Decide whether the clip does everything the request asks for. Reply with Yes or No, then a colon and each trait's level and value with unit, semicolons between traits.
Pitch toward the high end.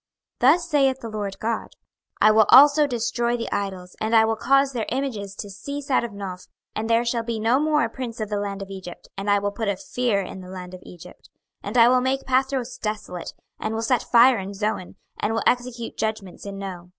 Yes: high, 225 Hz